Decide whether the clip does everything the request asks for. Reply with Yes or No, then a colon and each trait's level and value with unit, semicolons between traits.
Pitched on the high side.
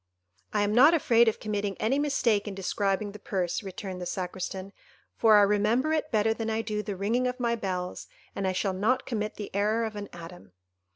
Yes: high, 210 Hz